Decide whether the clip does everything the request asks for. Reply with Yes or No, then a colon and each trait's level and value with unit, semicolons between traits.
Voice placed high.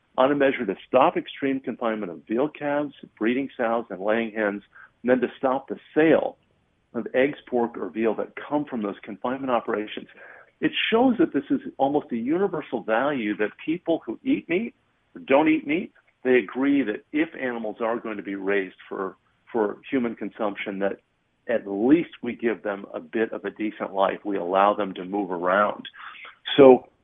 No: low, 120 Hz